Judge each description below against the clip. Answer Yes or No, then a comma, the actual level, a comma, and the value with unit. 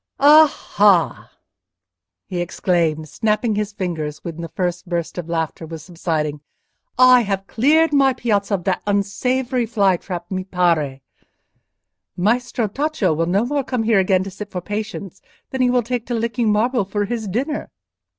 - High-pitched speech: Yes, high, 200 Hz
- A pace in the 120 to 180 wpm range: Yes, average, 160 wpm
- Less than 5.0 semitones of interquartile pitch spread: No, wide, 5.5 semitones